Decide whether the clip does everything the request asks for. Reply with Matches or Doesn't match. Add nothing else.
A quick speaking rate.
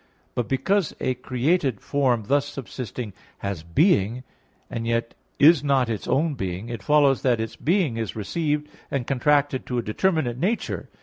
Doesn't match